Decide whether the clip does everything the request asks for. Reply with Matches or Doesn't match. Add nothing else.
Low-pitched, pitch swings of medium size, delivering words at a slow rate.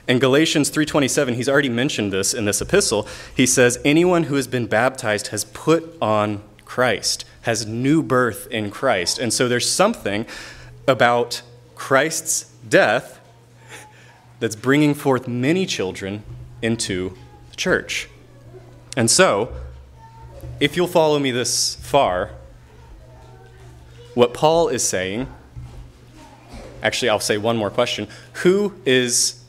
Matches